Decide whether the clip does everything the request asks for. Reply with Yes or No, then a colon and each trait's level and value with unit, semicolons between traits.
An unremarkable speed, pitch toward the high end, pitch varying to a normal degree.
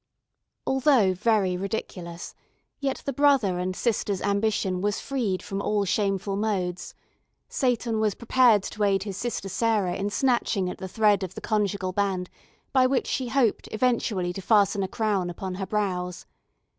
Yes: average, 155 wpm; high, 200 Hz; average, 3.3 semitones